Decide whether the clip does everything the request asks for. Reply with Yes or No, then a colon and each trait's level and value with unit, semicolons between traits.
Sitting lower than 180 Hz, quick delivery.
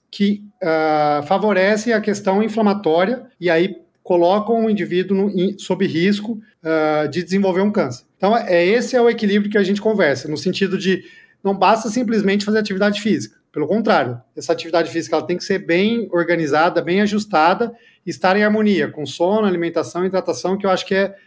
No: high, 190 Hz; fast, 190 wpm